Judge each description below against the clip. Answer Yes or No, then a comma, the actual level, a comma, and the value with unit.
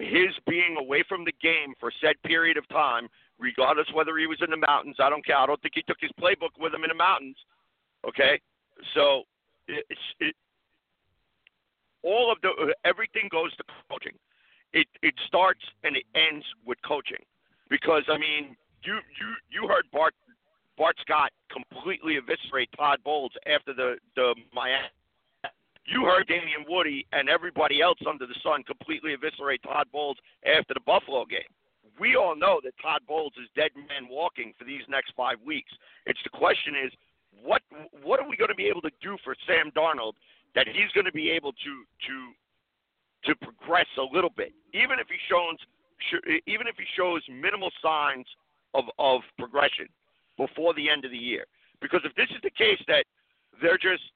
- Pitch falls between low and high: Yes, medium, 165 Hz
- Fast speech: No, average, 180 wpm